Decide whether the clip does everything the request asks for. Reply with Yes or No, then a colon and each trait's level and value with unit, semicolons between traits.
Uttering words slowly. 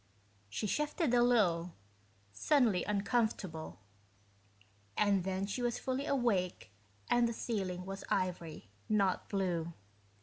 Yes: slow, 110 wpm